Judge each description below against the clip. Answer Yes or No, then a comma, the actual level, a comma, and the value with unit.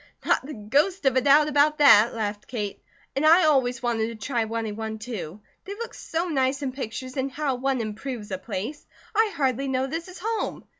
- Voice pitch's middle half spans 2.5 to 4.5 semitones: No, average, 5.0 semitones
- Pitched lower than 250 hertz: No, very high, 260 Hz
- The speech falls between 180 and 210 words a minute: Yes, fast, 205 wpm